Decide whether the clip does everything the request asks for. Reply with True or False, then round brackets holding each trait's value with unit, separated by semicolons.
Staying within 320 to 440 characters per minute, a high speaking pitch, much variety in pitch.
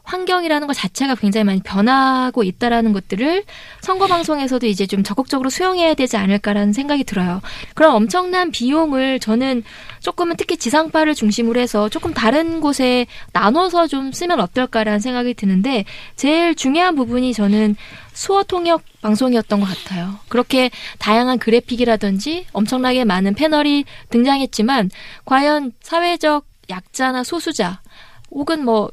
True (350 characters per minute; 255 Hz; 6.3 semitones)